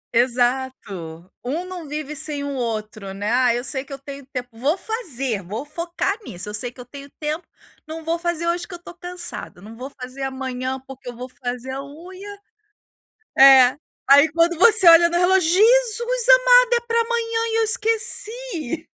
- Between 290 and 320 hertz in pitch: Yes, very high, 295 Hz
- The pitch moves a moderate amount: No, wide, 6.5 semitones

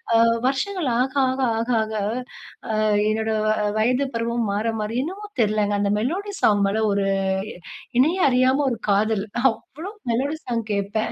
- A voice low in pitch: No, high, 230 Hz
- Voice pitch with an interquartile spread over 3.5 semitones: Yes, average, 4.0 semitones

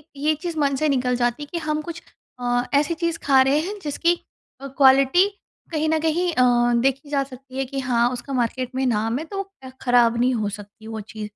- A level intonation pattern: No, average, 3.9 semitones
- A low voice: No, very high, 265 Hz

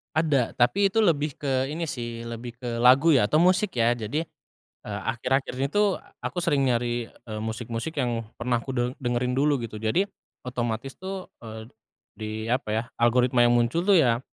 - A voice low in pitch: Yes, low, 125 Hz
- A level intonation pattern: No, average, 4.2 semitones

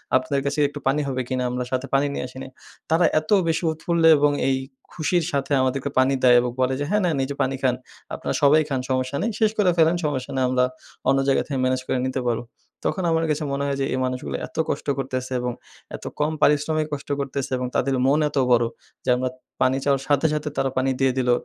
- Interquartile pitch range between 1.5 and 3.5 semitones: Yes, narrow, 2.5 semitones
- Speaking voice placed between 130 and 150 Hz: Yes, low, 135 Hz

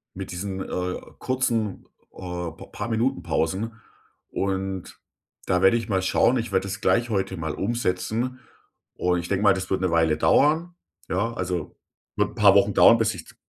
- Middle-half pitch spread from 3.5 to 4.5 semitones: Yes, average, 3.8 semitones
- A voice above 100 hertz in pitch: No, very low, 95 Hz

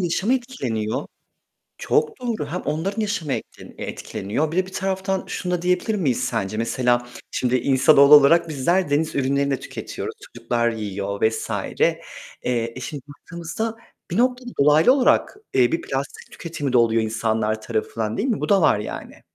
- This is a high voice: No, medium, 145 Hz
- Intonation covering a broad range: Yes, wide, 7.7 semitones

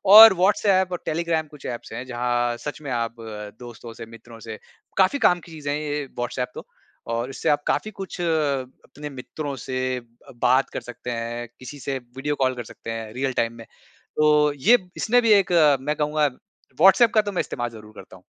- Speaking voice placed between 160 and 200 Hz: No, low, 135 Hz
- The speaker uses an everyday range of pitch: Yes, average, 4.8 semitones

